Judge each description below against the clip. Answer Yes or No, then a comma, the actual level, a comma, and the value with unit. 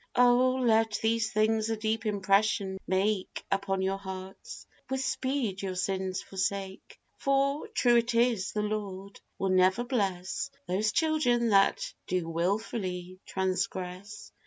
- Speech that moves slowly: Yes, slow, 130 wpm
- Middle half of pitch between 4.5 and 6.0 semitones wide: No, average, 3.5 semitones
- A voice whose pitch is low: No, high, 200 Hz